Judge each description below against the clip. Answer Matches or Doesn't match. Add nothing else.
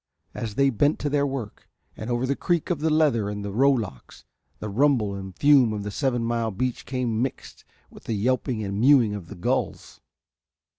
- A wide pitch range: Doesn't match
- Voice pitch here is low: Matches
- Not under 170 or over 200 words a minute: Matches